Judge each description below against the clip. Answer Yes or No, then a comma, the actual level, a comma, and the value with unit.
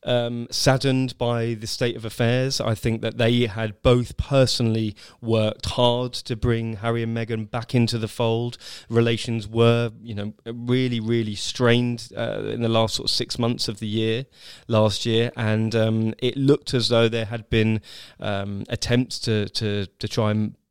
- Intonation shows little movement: Yes, narrow, 1.6 semitones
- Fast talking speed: No, average, 175 wpm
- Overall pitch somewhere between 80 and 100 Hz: No, low, 115 Hz